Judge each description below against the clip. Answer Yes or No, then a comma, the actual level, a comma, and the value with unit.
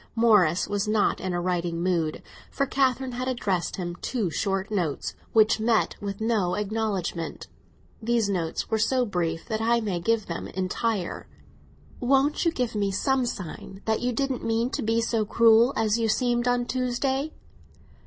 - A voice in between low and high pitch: No, high, 220 Hz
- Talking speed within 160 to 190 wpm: Yes, average, 165 wpm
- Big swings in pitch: No, average, 4.3 semitones